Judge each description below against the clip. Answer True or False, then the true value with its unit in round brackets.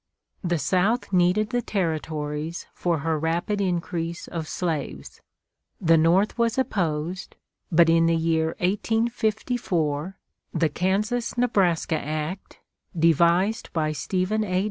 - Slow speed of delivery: True (115 wpm)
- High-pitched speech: False (175 Hz)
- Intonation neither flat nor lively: True (3.8 semitones)